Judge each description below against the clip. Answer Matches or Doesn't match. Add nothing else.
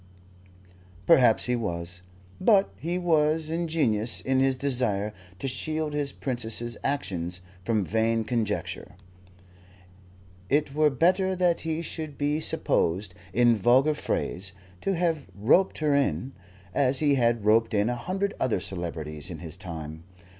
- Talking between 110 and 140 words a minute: Matches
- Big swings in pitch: Matches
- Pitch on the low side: Matches